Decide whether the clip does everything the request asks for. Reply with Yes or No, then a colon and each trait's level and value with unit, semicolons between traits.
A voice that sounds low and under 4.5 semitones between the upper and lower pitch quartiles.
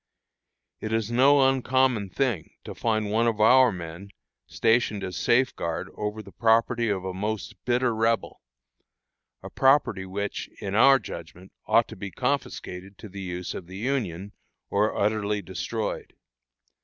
Yes: low, 110 Hz; average, 3.8 semitones